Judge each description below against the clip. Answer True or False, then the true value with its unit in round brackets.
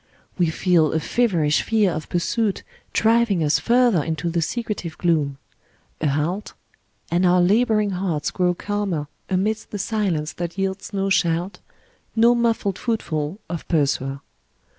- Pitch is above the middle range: False (180 Hz)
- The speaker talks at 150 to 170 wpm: False (140 wpm)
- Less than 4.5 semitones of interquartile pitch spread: False (4.8 semitones)